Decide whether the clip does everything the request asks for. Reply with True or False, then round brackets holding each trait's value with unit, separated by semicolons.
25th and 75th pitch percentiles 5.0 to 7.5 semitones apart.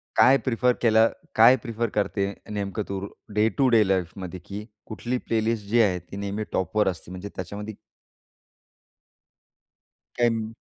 False (2.8 semitones)